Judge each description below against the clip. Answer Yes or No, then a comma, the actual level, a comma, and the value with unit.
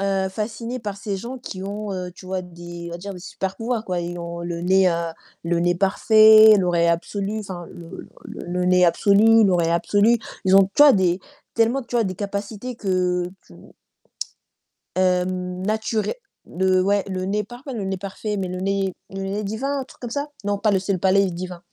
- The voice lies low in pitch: No, high, 195 Hz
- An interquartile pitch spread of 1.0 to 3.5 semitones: Yes, average, 2.8 semitones